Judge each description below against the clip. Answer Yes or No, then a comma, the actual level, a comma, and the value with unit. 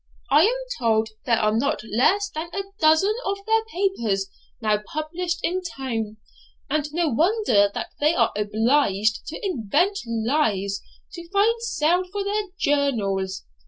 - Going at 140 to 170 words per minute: Yes, average, 145 wpm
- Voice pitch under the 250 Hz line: No, very high, 295 Hz